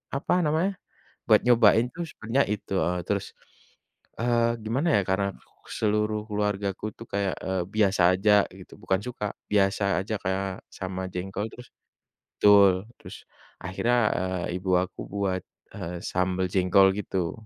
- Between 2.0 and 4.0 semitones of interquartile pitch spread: Yes, average, 2.8 semitones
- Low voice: Yes, low, 100 Hz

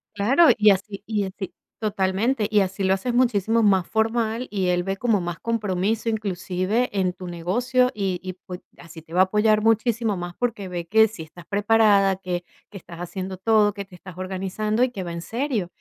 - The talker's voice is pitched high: Yes, high, 200 Hz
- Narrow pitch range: No, average, 3.2 semitones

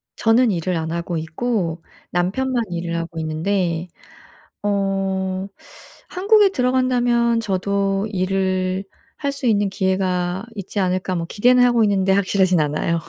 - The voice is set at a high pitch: Yes, high, 195 Hz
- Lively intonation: No, average, 4.2 semitones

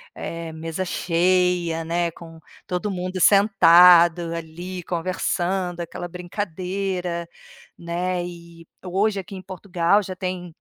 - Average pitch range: No, narrow, 1.6 semitones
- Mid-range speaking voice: Yes, medium, 180 Hz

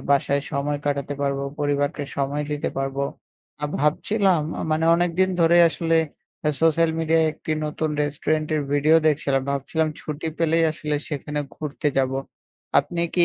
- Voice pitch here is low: No, medium, 150 Hz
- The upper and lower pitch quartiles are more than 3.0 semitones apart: No, narrow, 2.4 semitones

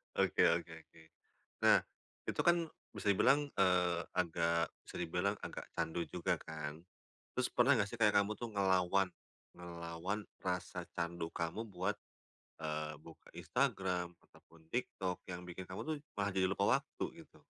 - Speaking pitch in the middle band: No, very low, 90 Hz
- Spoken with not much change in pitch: No, average, 3.2 semitones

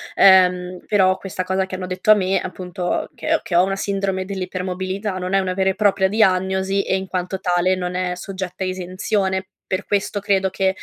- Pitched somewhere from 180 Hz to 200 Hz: Yes, high, 190 Hz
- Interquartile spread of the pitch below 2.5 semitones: Yes, narrow, 1.0 semitones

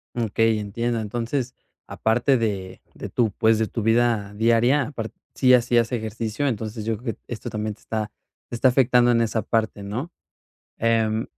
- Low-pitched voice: Yes, low, 115 Hz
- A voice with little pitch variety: Yes, narrow, 1.8 semitones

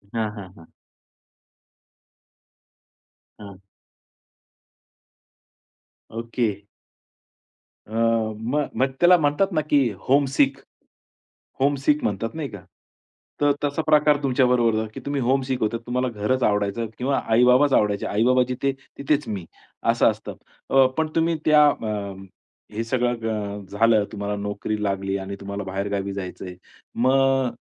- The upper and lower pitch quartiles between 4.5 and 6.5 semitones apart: Yes, average, 5.0 semitones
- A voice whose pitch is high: No, low, 120 Hz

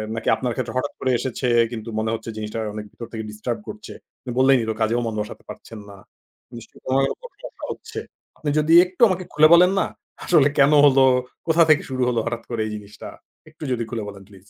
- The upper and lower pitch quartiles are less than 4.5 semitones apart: No, wide, 5.4 semitones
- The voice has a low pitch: Yes, low, 120 Hz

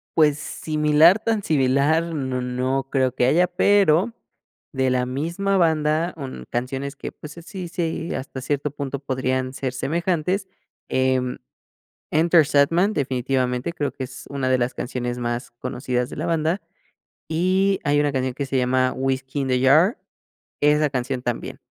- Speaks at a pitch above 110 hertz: Yes, medium, 140 Hz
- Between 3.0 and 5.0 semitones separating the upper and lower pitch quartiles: Yes, average, 4.0 semitones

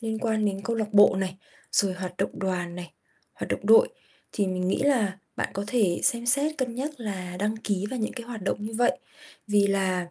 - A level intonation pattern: No, average, 3.9 semitones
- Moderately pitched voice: No, high, 205 Hz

